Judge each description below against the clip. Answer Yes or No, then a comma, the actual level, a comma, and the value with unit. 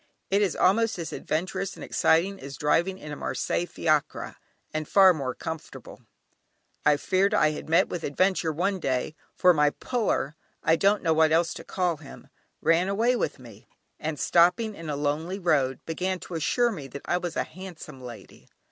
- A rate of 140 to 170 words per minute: No, average, 185 wpm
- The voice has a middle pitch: Yes, medium, 165 Hz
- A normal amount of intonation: Yes, average, 4.0 semitones